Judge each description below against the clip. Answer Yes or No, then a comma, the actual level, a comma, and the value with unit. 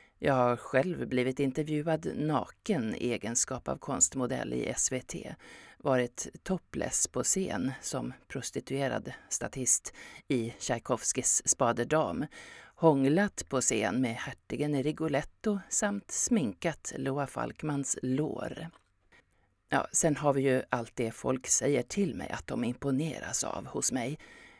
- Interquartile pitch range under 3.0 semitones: No, average, 4.0 semitones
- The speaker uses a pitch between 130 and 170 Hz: Yes, medium, 140 Hz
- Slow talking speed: Yes, slow, 120 wpm